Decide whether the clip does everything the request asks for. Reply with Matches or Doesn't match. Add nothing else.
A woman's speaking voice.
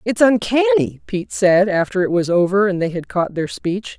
Matches